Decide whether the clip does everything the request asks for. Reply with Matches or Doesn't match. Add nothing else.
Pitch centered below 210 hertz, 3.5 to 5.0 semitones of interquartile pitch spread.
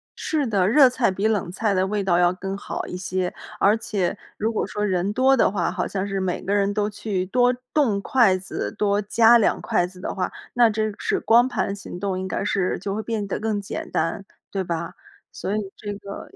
Doesn't match